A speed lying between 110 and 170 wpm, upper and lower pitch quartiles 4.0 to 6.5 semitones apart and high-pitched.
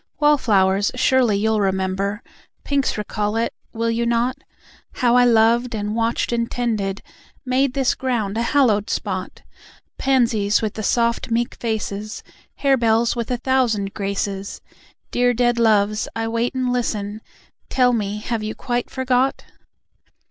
No: average, 140 wpm; average, 2.9 semitones; high, 230 Hz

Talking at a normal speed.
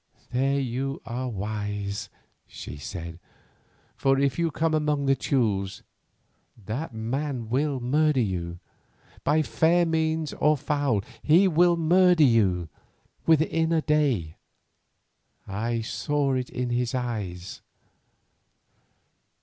No: slow, 110 wpm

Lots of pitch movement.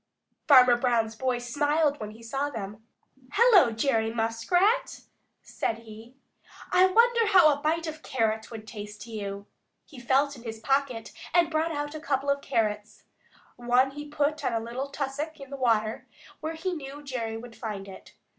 No: average, 4.8 semitones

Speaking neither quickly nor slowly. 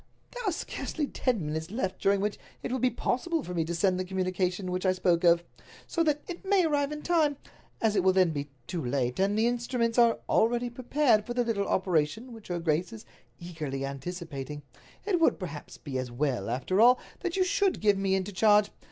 No: fast, 215 wpm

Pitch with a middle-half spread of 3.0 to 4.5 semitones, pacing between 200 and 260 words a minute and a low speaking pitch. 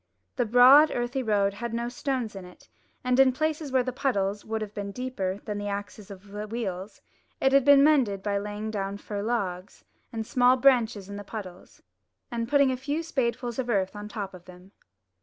No: average, 4.2 semitones; fast, 205 wpm; high, 220 Hz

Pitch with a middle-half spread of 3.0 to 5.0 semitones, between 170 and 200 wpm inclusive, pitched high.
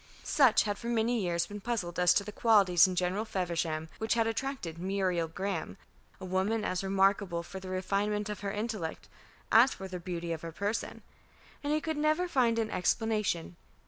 Yes: average, 3.9 semitones; average, 185 wpm; high, 195 Hz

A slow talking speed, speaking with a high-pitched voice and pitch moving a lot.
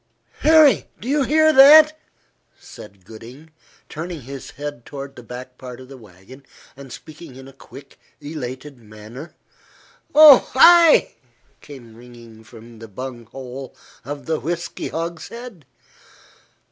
No: slow, 125 wpm; low, 135 Hz; wide, 5.9 semitones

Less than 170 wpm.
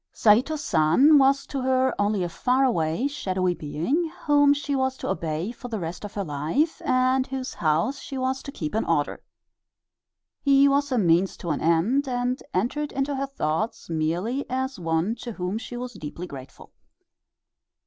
No: average, 175 wpm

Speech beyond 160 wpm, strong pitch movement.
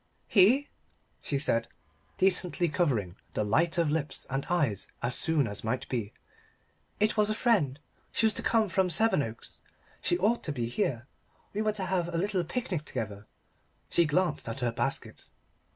Yes: average, 170 wpm; wide, 7.4 semitones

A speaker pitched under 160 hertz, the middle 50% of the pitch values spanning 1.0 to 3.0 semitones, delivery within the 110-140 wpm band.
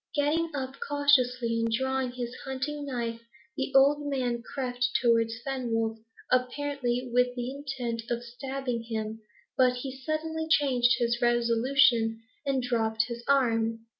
No: very high, 250 Hz; narrow, 2.6 semitones; slow, 135 wpm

